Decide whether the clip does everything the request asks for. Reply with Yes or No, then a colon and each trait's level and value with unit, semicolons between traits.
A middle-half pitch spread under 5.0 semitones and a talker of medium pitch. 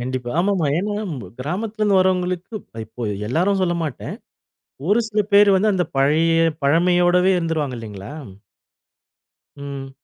No: wide, 5.5 semitones; medium, 170 Hz